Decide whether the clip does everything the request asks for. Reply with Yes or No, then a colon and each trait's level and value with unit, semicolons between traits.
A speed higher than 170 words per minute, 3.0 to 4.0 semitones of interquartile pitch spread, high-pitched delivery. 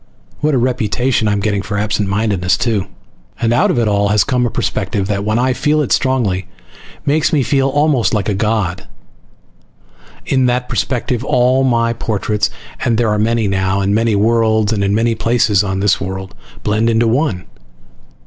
No: average, 180 wpm; average, 3.4 semitones; low, 110 Hz